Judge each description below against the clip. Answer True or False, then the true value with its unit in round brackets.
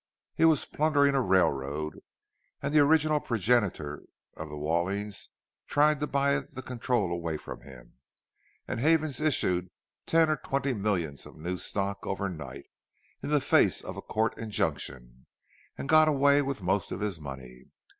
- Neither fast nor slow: True (155 wpm)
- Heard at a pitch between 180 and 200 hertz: False (105 Hz)